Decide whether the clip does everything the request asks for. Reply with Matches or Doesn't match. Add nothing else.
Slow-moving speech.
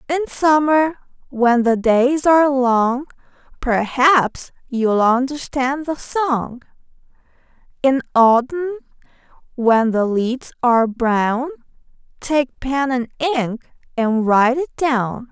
Matches